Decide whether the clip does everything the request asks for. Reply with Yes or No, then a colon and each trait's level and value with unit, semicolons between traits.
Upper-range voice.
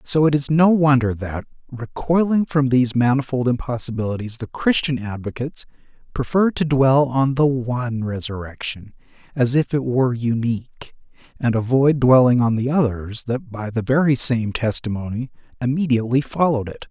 No: low, 130 Hz